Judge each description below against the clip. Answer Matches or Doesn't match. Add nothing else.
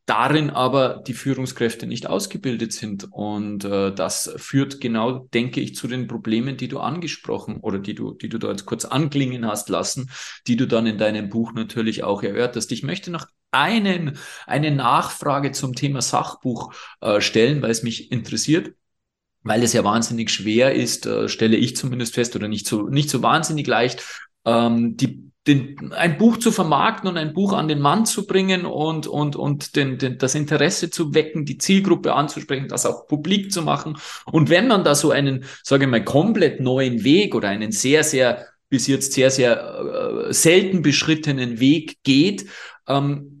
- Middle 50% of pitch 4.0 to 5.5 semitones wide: Matches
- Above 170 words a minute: Matches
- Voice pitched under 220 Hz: Matches